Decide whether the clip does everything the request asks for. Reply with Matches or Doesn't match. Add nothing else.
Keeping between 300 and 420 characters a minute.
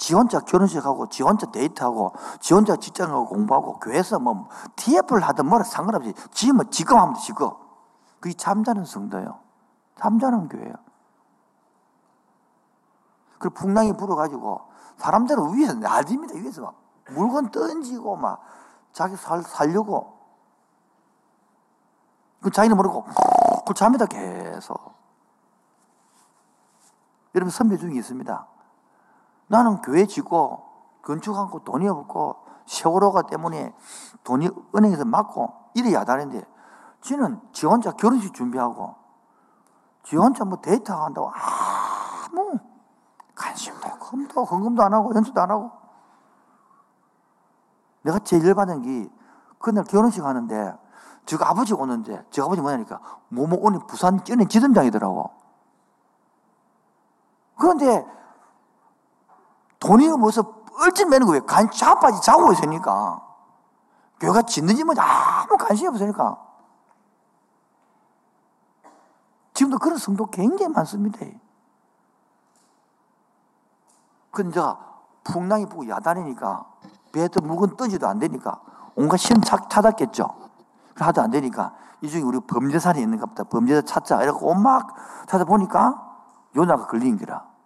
Doesn't match